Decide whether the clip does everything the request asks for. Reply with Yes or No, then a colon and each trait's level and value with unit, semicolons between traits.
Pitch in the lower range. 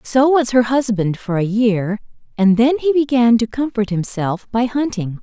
No: high, 230 Hz